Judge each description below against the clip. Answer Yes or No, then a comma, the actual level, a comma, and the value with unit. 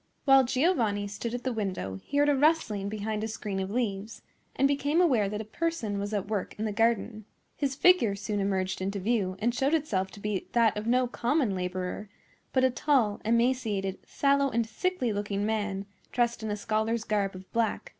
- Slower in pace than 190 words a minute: No, average, 195 wpm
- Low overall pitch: No, high, 220 Hz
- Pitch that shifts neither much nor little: Yes, average, 3.9 semitones